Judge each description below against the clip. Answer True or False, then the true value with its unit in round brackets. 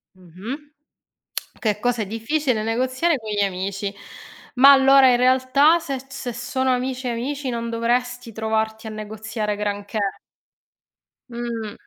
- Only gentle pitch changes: False (3.2 semitones)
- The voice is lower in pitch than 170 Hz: False (235 Hz)